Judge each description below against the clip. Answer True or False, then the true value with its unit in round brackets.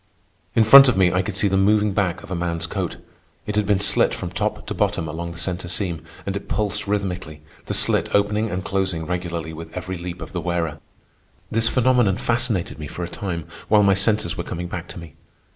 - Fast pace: True (220 wpm)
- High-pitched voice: False (95 Hz)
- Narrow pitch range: False (3.3 semitones)